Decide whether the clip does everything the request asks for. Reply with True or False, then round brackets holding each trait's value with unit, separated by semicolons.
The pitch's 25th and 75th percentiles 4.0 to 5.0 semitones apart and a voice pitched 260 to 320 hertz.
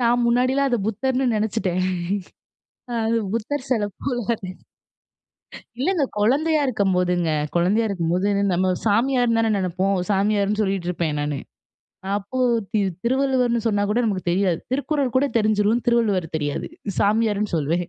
False (4.5 semitones; 215 Hz)